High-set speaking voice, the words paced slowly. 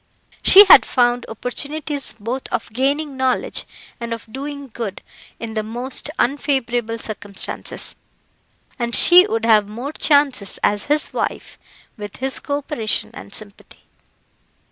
Yes: high, 245 Hz; slow, 130 wpm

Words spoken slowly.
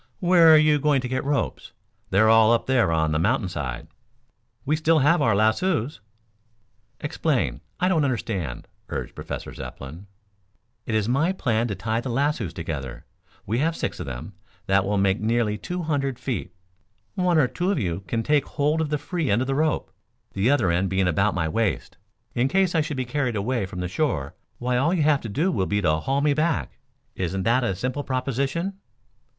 No: average, 195 wpm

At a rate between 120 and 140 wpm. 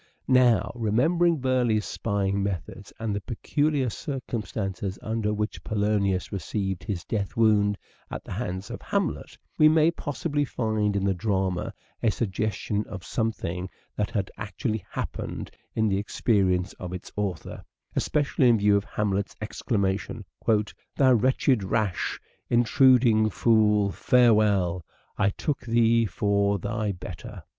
Yes: slow, 135 wpm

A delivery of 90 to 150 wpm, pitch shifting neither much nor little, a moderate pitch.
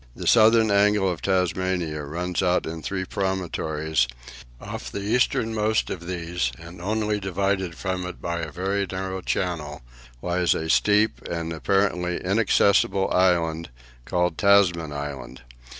No: slow, 135 wpm; average, 3.1 semitones; very low, 90 Hz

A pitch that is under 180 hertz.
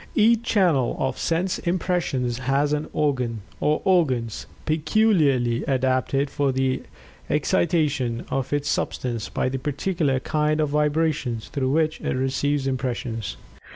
Yes: medium, 140 Hz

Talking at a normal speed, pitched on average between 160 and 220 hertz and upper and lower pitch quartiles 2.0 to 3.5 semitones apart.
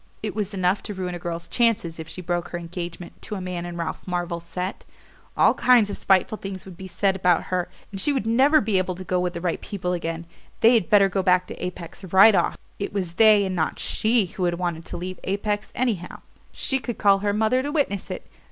No: fast, 235 wpm; medium, 185 Hz; average, 3.0 semitones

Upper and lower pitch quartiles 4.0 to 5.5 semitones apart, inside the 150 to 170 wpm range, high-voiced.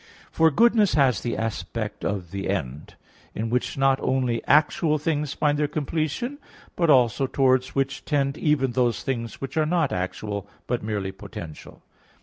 No: average, 5.2 semitones; average, 155 wpm; low, 135 Hz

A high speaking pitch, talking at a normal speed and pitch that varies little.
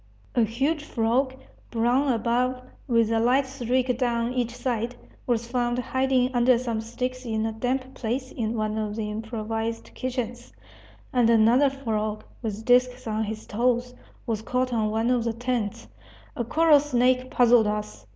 Yes: high, 240 Hz; average, 160 wpm; narrow, 2.3 semitones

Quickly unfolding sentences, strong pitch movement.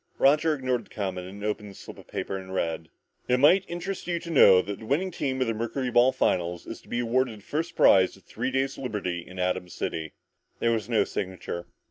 Yes: fast, 225 wpm; wide, 6.1 semitones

